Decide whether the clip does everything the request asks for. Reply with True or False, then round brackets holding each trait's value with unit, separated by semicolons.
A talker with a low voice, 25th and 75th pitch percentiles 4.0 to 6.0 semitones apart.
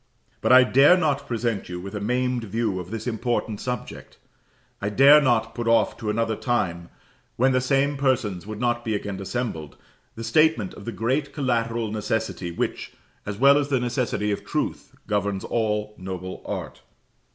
False (115 Hz; 3.6 semitones)